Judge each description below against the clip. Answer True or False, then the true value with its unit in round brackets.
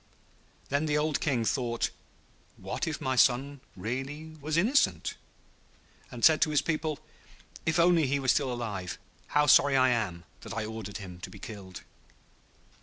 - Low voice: True (130 Hz)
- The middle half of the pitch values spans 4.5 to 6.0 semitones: True (5.3 semitones)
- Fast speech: False (160 wpm)